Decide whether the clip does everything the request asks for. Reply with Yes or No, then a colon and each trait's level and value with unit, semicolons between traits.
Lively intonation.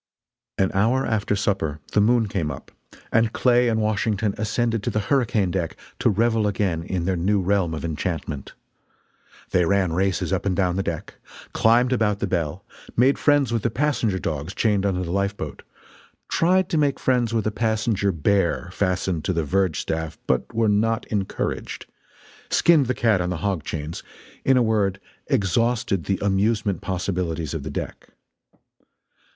No: average, 3.9 semitones